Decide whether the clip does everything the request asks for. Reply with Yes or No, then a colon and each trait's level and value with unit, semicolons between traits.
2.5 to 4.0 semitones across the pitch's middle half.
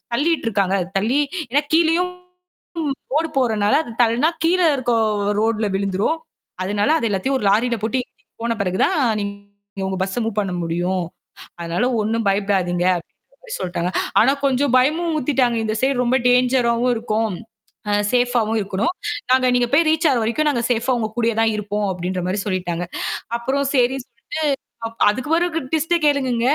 No: average, 4.7 semitones